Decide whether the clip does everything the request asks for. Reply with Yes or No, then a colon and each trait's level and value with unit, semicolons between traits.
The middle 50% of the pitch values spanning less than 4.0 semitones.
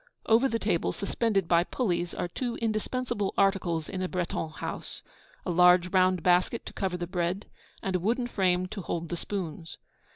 Yes: average, 3.1 semitones